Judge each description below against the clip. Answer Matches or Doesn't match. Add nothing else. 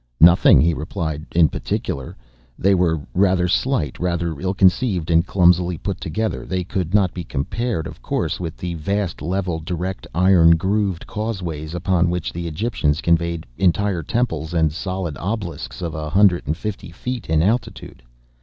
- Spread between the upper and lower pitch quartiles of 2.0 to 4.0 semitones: Matches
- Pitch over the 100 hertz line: Doesn't match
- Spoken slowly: Doesn't match